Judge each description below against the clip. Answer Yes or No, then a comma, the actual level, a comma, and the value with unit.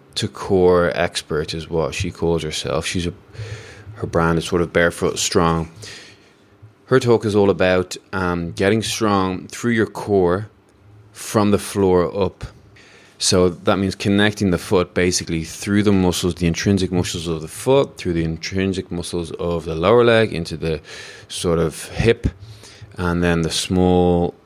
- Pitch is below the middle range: Yes, very low, 95 Hz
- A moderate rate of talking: Yes, average, 160 wpm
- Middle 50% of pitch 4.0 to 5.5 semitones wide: No, average, 3.1 semitones